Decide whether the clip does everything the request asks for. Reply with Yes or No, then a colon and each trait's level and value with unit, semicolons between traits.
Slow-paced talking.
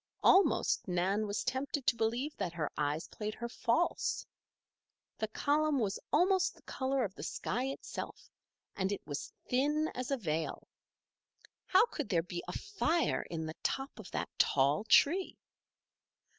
No: average, 155 wpm